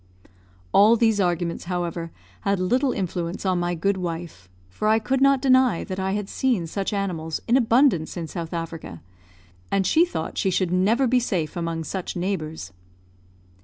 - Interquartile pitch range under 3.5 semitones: No, average, 4.8 semitones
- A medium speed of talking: Yes, average, 165 wpm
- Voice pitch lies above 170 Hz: Yes, medium, 185 Hz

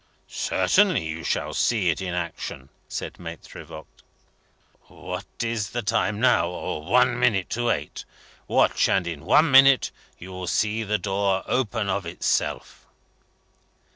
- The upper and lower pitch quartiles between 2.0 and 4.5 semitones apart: No, average, 5.2 semitones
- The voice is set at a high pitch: No, low, 105 Hz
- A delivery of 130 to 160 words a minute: Yes, average, 140 wpm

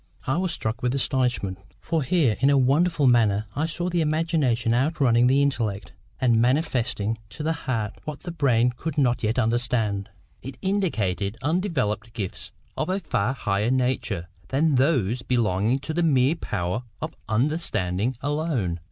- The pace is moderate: Yes, average, 160 wpm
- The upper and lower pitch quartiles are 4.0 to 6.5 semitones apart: Yes, wide, 5.5 semitones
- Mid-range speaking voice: No, low, 125 Hz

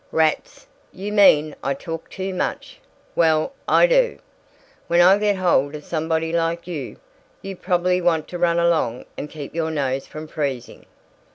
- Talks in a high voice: No, medium, 165 Hz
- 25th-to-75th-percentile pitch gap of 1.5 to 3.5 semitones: Yes, average, 2.9 semitones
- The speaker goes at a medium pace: Yes, average, 160 wpm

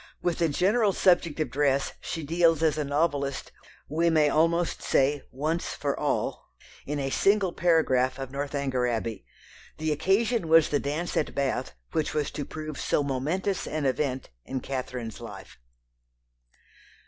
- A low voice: No, medium, 150 Hz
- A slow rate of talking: No, average, 150 wpm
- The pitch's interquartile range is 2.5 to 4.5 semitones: Yes, average, 3.4 semitones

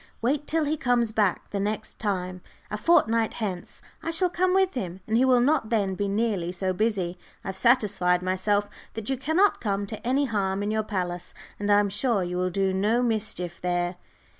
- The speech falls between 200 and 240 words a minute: Yes, fast, 205 wpm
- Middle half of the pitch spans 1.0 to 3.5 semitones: No, average, 4.4 semitones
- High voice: Yes, high, 210 Hz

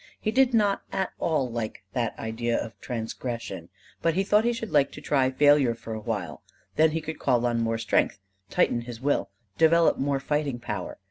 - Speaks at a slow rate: No, average, 195 wpm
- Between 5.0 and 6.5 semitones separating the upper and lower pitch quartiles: Yes, wide, 5.5 semitones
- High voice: No, low, 130 Hz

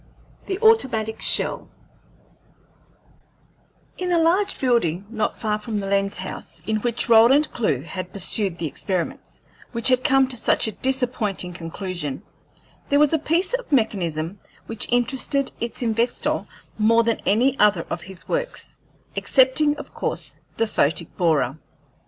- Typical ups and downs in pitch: No, wide, 5.9 semitones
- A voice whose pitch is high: Yes, high, 225 Hz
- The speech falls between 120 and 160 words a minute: Yes, average, 140 wpm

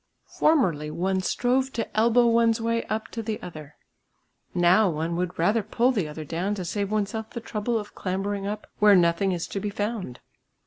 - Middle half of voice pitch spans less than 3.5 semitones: No, average, 4.3 semitones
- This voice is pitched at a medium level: No, high, 205 Hz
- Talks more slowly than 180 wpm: No, average, 185 wpm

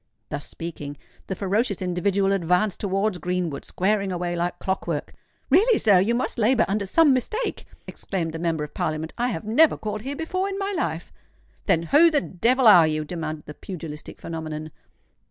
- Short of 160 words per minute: No, average, 175 wpm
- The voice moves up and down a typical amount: No, wide, 6.0 semitones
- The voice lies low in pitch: No, high, 190 Hz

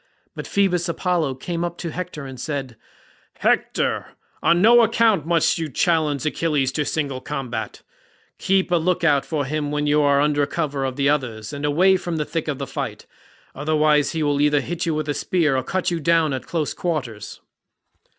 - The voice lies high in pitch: No, medium, 150 Hz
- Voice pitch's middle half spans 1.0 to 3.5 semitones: Yes, average, 3.2 semitones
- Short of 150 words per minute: No, average, 190 wpm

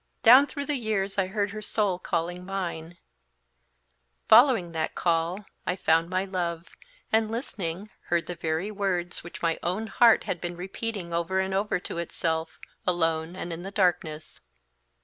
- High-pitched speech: No, medium, 180 Hz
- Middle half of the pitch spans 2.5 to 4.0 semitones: Yes, average, 3.2 semitones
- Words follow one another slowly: No, average, 160 wpm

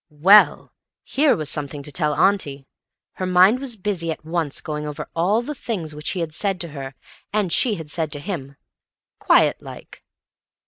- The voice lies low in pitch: No, medium, 165 Hz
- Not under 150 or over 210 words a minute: Yes, average, 175 wpm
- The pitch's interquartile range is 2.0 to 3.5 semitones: No, average, 5.1 semitones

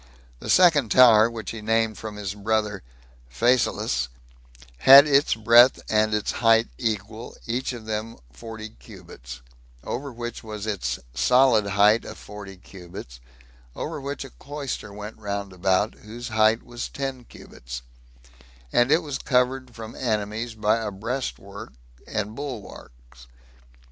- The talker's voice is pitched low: Yes, low, 110 Hz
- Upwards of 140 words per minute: No, slow, 135 wpm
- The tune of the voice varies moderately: Yes, average, 3.0 semitones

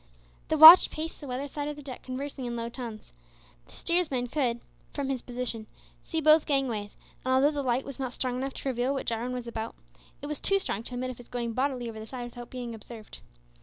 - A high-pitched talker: Yes, very high, 255 Hz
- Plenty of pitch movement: No, average, 2.9 semitones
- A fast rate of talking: Yes, fast, 230 wpm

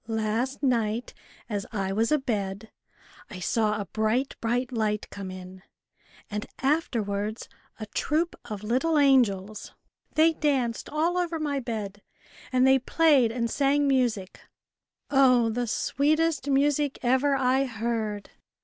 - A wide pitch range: No, average, 4.6 semitones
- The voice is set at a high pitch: Yes, high, 240 Hz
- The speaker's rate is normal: No, slow, 130 wpm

